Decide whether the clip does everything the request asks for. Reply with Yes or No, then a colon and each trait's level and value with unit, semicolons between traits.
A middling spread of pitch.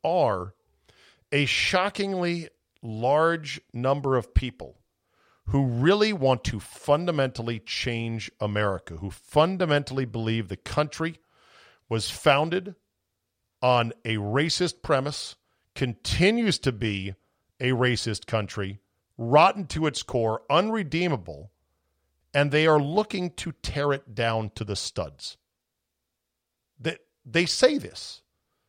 No: wide, 6.7 semitones